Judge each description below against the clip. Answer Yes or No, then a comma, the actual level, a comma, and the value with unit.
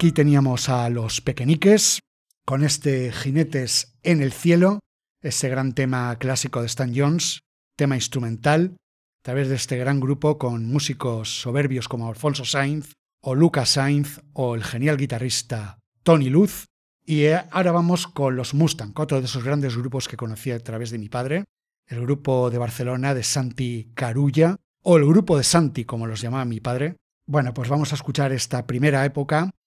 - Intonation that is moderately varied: Yes, average, 3.4 semitones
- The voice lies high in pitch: No, low, 135 Hz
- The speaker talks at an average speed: Yes, average, 170 wpm